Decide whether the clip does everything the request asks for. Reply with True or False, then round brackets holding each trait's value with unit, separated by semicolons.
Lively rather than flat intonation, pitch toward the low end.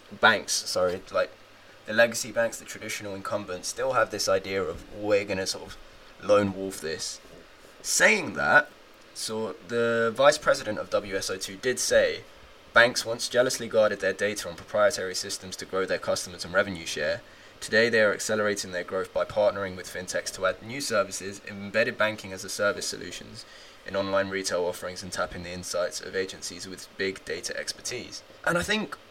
False (2.6 semitones; 100 Hz)